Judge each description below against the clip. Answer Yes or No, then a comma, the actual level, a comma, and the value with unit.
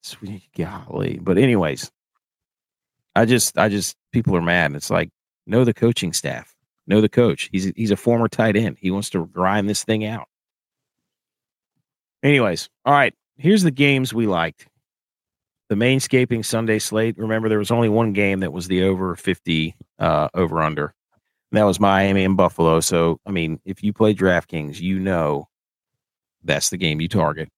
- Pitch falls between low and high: No, low, 100 Hz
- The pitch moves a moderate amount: Yes, average, 3.6 semitones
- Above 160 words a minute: Yes, average, 170 wpm